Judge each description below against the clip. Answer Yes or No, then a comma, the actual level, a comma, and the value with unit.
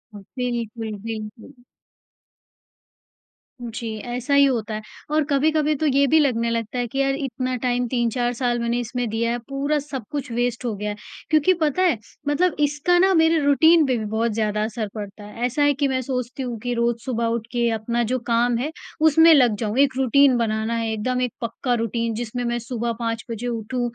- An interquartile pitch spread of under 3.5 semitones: Yes, average, 3.1 semitones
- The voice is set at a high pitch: Yes, high, 245 Hz